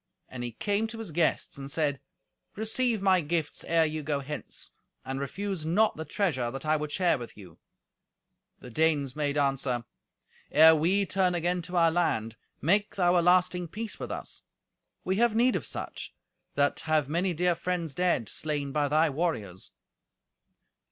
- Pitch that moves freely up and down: No, average, 4.3 semitones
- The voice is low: No, medium, 160 Hz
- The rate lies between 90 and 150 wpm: No, average, 170 wpm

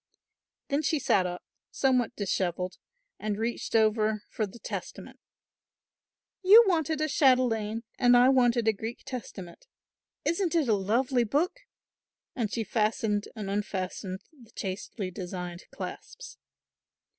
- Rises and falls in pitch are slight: No, average, 4.7 semitones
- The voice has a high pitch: Yes, high, 225 Hz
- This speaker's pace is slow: Yes, slow, 125 wpm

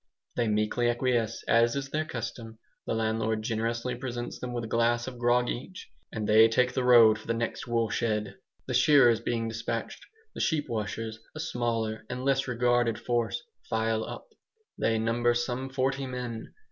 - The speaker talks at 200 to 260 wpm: No, average, 170 wpm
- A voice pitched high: No, low, 120 Hz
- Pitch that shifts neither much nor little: No, narrow, 1.8 semitones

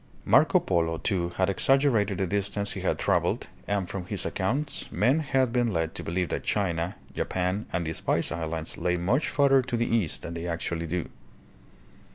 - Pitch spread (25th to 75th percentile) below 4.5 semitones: No, wide, 5.5 semitones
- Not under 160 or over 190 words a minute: Yes, average, 185 wpm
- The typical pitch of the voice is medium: No, very low, 95 Hz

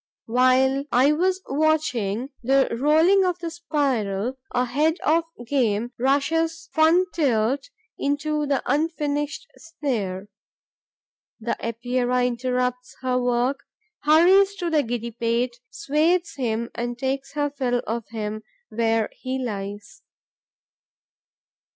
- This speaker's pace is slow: Yes, slow, 115 wpm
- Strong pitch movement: No, average, 4.4 semitones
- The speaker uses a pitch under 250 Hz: No, very high, 265 Hz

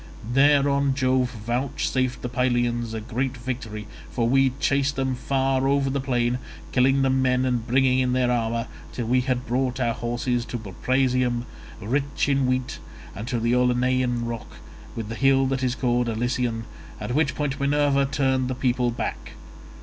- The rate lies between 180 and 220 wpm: No, average, 165 wpm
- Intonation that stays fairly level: Yes, narrow, 1.8 semitones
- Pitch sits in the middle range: No, low, 125 Hz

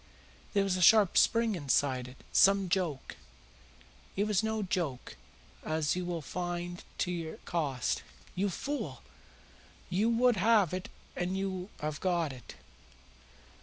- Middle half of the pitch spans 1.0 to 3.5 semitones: No, average, 4.0 semitones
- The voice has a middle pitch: Yes, medium, 180 Hz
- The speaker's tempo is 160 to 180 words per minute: No, average, 140 wpm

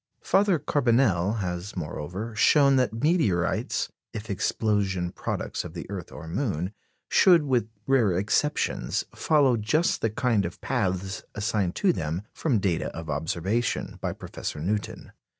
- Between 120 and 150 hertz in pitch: No, low, 105 Hz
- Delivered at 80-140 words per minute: Yes, slow, 135 wpm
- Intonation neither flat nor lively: No, wide, 6.4 semitones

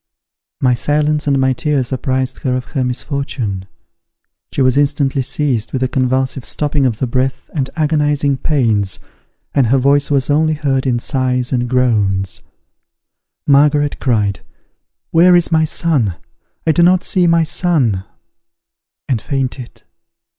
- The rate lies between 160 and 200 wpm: No, average, 140 wpm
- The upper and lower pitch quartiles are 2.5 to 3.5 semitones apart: Yes, average, 2.8 semitones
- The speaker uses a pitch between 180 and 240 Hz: No, low, 135 Hz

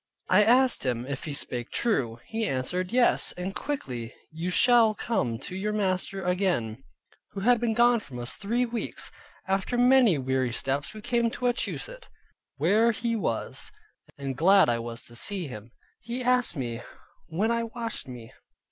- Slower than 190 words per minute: Yes, average, 165 wpm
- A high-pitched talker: Yes, high, 195 Hz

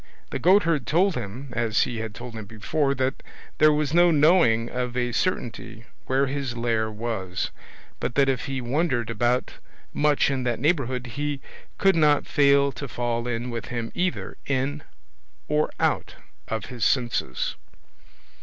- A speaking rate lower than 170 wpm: Yes, average, 155 wpm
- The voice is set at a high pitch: No, low, 125 Hz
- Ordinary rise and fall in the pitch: Yes, average, 3.8 semitones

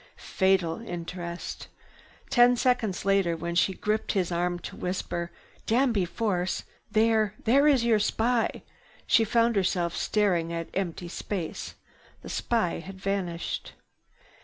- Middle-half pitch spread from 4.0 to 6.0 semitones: Yes, average, 4.4 semitones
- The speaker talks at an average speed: No, slow, 120 wpm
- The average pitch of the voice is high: Yes, high, 195 Hz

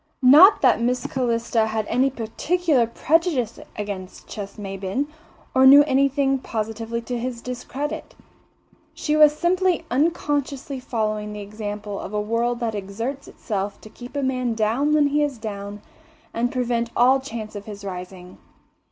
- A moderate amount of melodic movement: Yes, average, 4.4 semitones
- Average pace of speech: Yes, average, 150 wpm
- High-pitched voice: Yes, high, 235 Hz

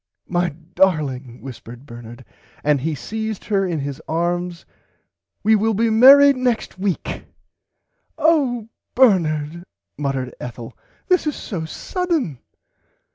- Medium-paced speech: No, slow, 115 wpm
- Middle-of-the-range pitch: Yes, medium, 175 Hz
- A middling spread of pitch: No, wide, 7.8 semitones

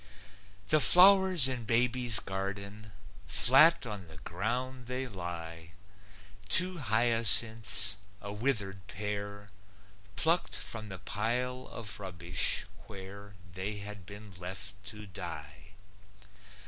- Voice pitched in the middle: No, low, 105 Hz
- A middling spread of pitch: Yes, average, 4.1 semitones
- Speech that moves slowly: Yes, slow, 105 wpm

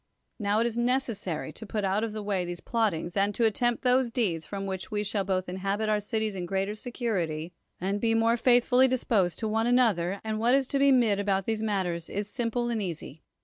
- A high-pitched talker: Yes, high, 210 Hz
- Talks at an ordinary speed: No, fast, 230 wpm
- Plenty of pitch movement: No, average, 3.3 semitones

